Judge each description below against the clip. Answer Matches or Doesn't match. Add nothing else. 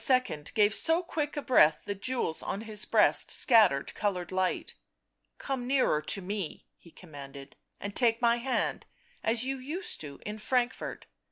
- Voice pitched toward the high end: Matches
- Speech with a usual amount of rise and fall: Doesn't match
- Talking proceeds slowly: Doesn't match